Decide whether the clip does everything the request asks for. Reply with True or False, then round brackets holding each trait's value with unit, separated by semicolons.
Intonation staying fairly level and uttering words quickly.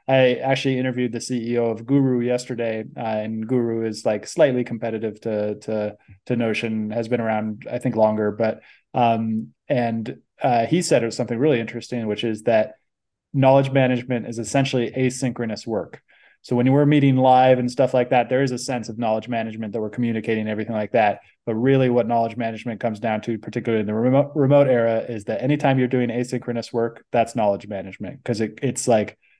False (2.3 semitones; 195 wpm)